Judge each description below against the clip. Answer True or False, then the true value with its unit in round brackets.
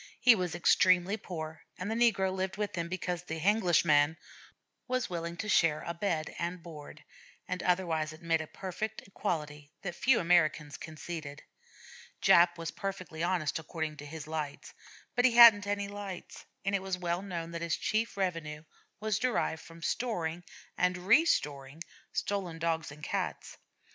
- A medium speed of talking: True (160 wpm)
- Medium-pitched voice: True (175 Hz)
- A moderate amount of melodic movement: True (3.6 semitones)